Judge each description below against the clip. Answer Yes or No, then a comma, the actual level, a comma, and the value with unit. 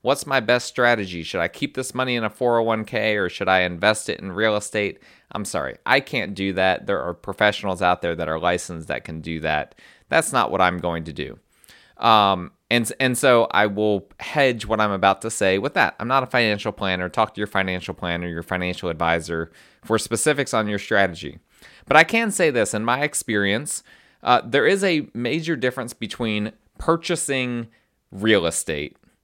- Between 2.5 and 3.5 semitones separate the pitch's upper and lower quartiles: No, average, 5.1 semitones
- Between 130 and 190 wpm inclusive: No, average, 200 wpm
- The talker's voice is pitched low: Yes, low, 105 Hz